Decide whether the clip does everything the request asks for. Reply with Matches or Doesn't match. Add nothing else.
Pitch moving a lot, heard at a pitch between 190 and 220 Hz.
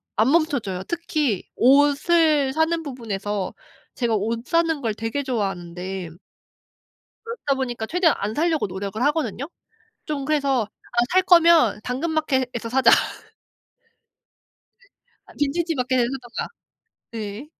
Doesn't match